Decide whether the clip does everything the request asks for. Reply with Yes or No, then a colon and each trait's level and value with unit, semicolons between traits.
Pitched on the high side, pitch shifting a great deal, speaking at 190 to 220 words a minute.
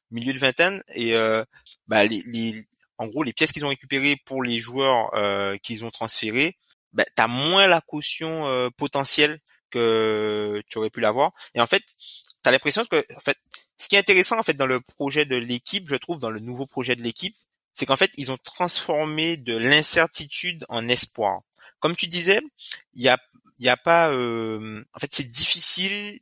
No: low, 135 Hz; wide, 6.0 semitones; average, 200 wpm